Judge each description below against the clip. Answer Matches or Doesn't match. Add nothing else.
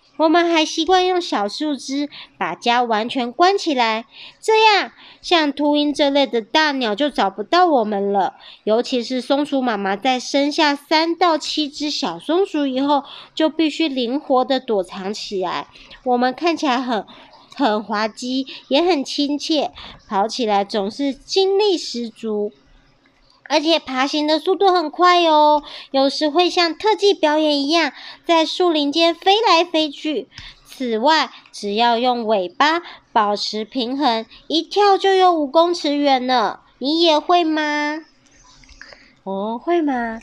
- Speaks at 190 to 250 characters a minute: Matches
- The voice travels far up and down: Doesn't match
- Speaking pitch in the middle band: Doesn't match